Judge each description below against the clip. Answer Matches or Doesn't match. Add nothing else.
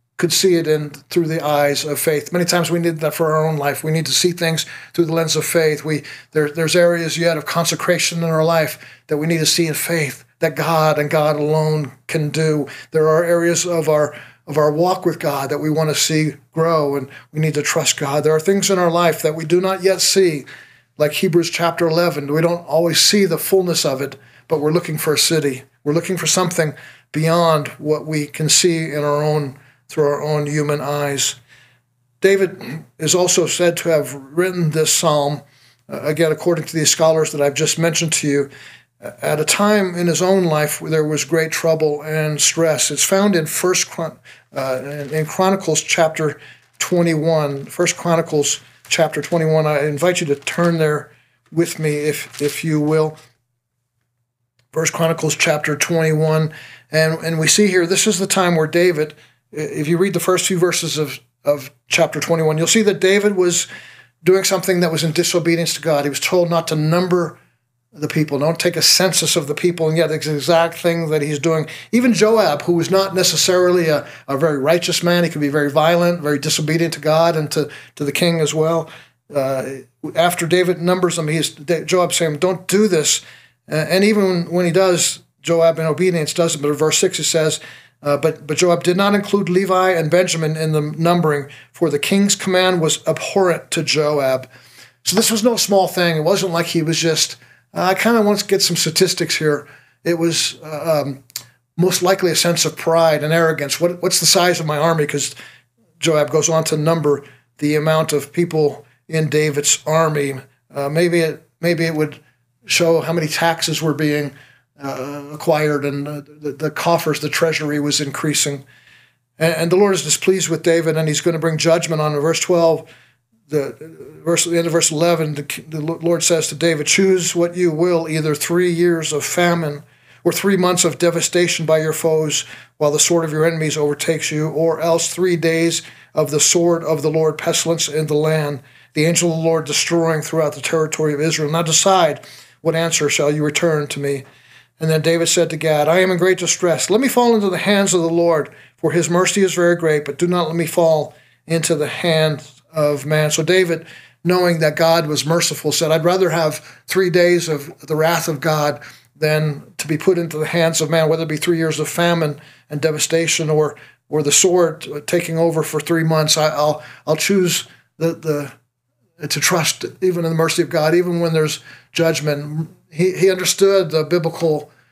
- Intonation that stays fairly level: Matches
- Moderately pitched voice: Matches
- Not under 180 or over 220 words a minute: Matches